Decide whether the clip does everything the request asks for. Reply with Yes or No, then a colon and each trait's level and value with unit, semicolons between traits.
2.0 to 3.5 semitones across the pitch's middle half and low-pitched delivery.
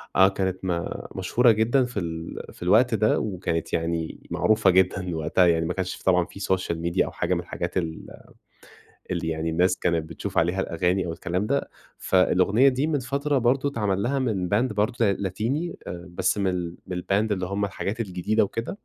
No: average, 4.1 semitones; very low, 95 Hz